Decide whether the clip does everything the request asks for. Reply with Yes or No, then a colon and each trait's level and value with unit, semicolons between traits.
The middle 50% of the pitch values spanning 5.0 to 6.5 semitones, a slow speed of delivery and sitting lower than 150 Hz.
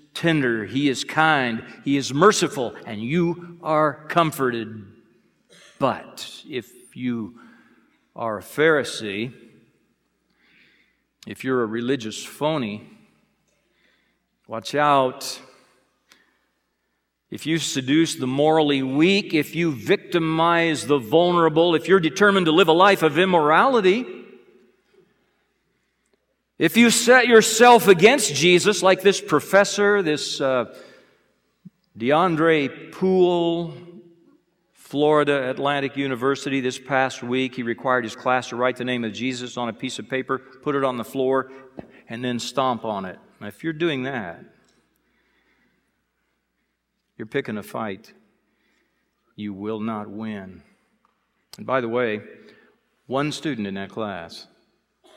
Yes: average, 5.3 semitones; slow, 120 wpm; medium, 140 Hz